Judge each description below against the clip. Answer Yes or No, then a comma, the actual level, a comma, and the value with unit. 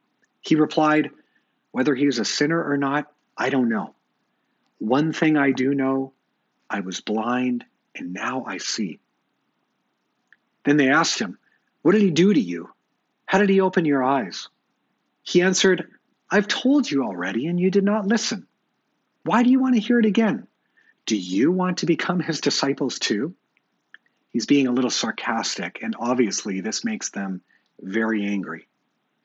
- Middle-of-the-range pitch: Yes, medium, 155 Hz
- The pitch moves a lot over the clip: Yes, wide, 7.5 semitones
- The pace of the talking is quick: No, average, 160 wpm